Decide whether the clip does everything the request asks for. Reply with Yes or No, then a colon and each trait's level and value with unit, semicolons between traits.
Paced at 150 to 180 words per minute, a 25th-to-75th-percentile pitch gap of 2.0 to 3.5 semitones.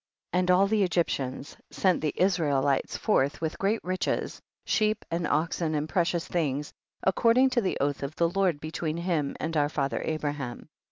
No: average, 175 wpm; average, 4.1 semitones